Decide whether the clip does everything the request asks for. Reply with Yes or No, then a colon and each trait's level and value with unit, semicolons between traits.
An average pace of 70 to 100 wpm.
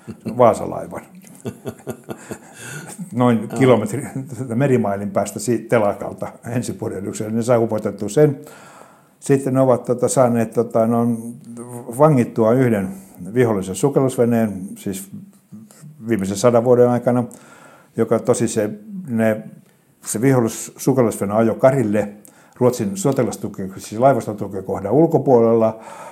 Yes: slow, 95 wpm